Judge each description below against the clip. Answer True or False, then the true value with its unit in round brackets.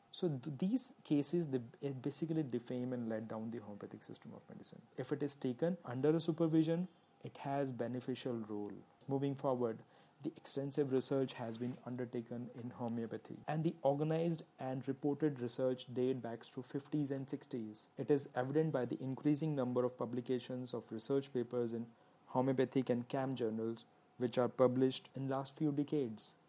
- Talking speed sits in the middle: True (165 wpm)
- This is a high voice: False (130 Hz)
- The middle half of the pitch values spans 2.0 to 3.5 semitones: True (3.0 semitones)